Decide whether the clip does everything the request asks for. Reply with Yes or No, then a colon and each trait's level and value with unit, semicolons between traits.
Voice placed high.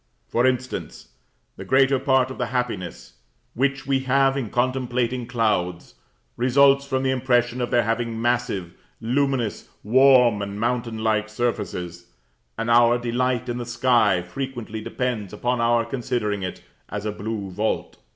No: low, 120 Hz